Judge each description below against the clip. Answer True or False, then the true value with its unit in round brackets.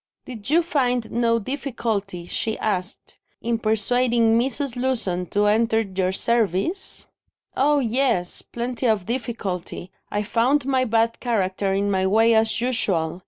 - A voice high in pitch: True (225 Hz)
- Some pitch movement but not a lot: True (3.8 semitones)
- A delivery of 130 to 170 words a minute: True (135 wpm)